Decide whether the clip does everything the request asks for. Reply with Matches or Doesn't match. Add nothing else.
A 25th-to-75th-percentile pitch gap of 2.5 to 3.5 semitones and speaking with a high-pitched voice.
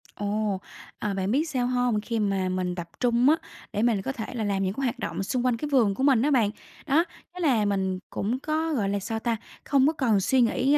Doesn't match